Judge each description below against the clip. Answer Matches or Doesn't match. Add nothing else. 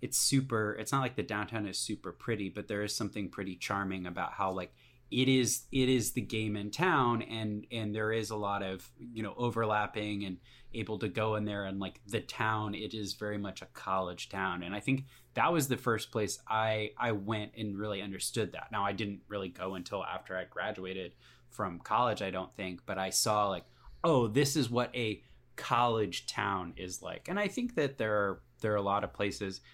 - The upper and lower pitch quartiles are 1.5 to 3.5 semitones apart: Matches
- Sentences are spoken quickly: Matches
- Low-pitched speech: Matches